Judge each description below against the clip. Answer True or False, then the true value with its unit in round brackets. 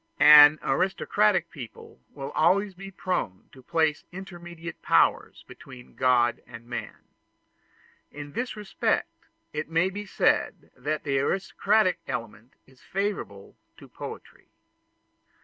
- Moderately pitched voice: True (155 Hz)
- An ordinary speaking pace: False (115 wpm)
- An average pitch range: False (6.4 semitones)